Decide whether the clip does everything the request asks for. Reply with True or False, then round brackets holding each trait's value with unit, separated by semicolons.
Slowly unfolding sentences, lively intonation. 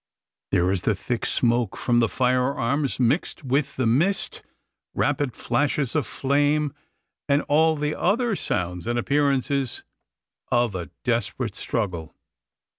False (125 wpm; 3.9 semitones)